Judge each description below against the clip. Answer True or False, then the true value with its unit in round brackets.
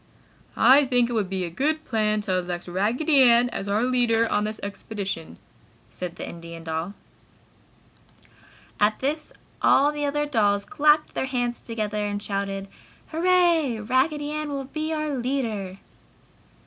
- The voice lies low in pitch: False (235 Hz)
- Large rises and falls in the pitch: True (6.2 semitones)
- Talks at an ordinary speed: True (150 wpm)